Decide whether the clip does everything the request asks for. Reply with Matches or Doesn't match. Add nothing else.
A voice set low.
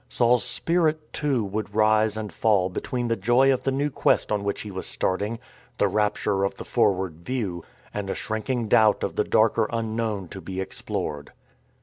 Matches